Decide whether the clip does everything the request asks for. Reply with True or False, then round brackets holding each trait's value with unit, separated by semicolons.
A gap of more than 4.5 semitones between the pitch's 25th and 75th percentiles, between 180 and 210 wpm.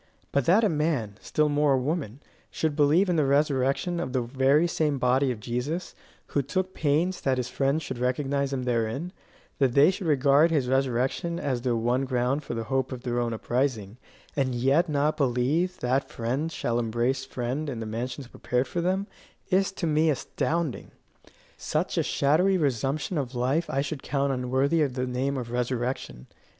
False (3.6 semitones; 185 wpm)